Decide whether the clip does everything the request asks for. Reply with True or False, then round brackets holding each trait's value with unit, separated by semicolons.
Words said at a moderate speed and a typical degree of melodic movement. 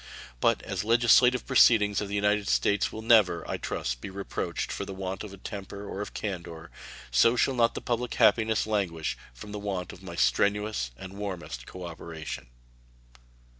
True (170 wpm; 3.6 semitones)